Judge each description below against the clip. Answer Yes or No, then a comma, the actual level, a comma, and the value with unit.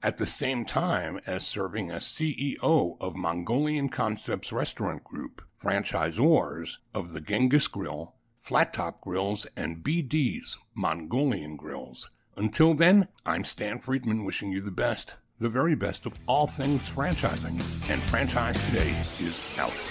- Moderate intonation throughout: No, wide, 6.7 semitones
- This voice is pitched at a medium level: No, low, 110 Hz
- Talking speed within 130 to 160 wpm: Yes, average, 140 wpm